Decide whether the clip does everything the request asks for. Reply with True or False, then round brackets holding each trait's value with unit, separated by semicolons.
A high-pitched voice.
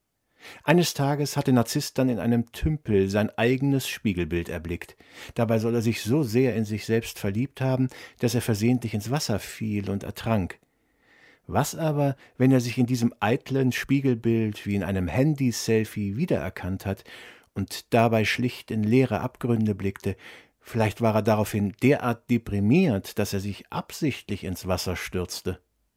False (115 Hz)